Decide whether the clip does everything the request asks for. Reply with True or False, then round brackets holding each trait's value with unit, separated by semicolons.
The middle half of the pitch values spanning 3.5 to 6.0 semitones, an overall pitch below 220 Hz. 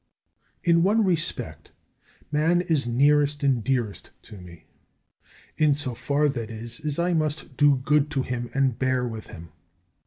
True (4.1 semitones; 140 Hz)